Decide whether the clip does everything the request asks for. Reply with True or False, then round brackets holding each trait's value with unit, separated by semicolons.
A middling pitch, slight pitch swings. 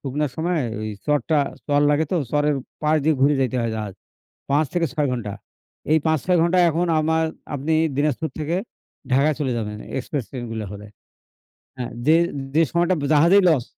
False (150 Hz; 3.8 semitones)